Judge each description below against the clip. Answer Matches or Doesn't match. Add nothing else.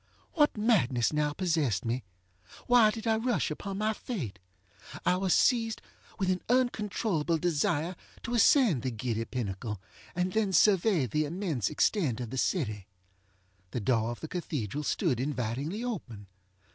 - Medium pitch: Matches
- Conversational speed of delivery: Matches